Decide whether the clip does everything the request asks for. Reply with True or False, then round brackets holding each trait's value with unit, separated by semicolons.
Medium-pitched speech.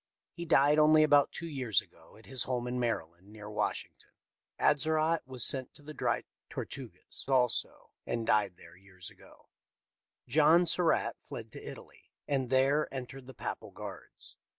False (130 Hz)